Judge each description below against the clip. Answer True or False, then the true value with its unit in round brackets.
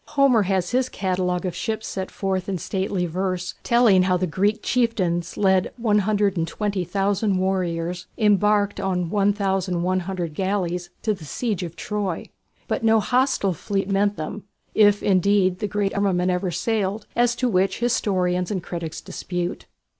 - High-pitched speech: True (195 Hz)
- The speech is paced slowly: False (145 wpm)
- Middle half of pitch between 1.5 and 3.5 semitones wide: True (2.4 semitones)